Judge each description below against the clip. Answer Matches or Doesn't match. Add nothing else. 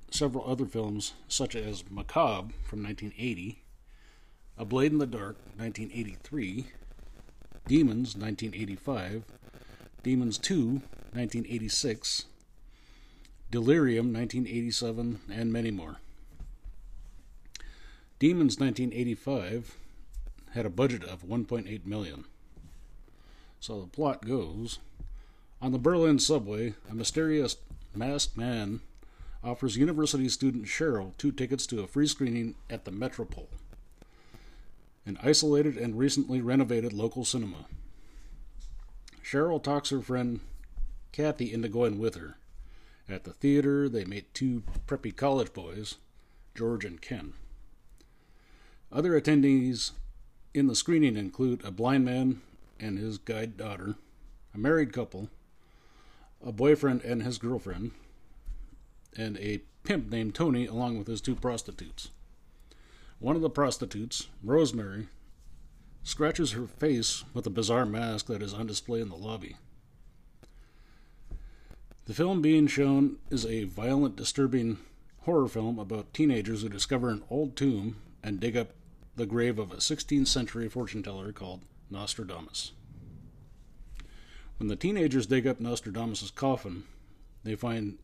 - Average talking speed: Doesn't match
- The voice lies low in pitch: Matches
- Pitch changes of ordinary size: Matches